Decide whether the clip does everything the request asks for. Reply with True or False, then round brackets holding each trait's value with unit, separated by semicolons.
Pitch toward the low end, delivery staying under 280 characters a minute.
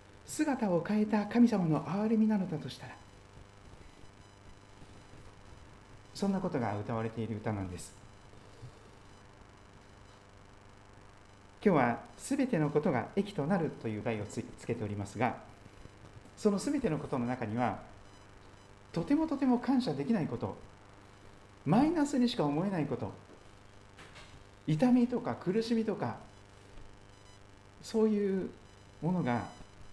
True (100 Hz; 235 characters per minute)